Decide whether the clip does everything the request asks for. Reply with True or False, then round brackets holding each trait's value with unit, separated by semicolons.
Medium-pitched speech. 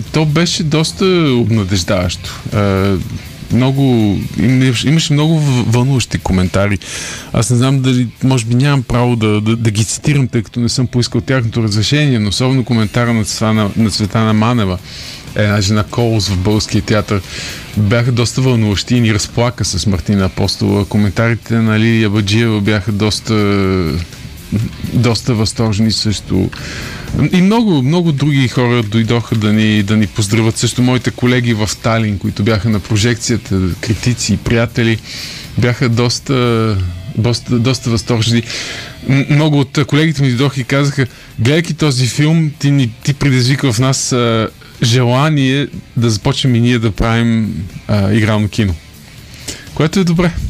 False (115 Hz)